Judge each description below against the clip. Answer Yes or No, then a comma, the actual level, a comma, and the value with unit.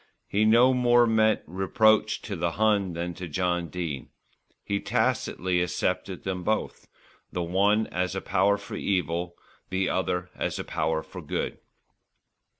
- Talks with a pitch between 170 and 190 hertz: No, very low, 95 Hz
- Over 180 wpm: No, average, 150 wpm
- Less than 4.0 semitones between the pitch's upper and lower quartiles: Yes, average, 3.4 semitones